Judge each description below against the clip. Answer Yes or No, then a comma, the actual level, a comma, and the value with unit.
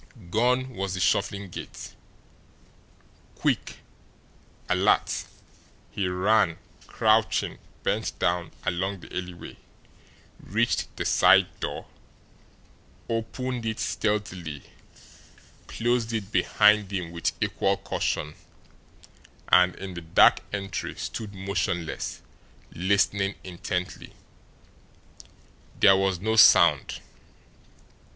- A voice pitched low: Yes, very low, 95 Hz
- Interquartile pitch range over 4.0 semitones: No, average, 3.1 semitones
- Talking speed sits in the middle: No, slow, 90 wpm